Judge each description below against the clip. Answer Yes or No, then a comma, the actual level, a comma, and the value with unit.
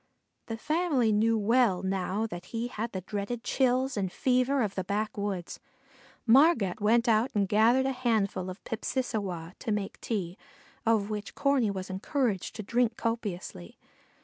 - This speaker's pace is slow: No, average, 150 wpm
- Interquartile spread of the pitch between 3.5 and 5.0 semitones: Yes, average, 3.8 semitones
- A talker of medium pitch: No, high, 220 Hz